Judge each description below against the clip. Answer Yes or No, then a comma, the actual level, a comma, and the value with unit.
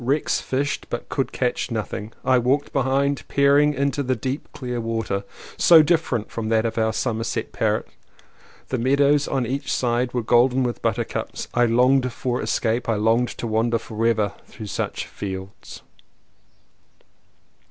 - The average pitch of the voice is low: Yes, low, 125 Hz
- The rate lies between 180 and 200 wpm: No, average, 150 wpm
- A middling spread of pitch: Yes, average, 3.2 semitones